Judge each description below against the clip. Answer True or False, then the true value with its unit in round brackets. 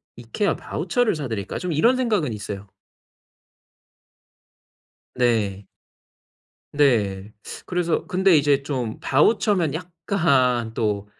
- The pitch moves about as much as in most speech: False (8.2 semitones)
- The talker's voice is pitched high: False (140 Hz)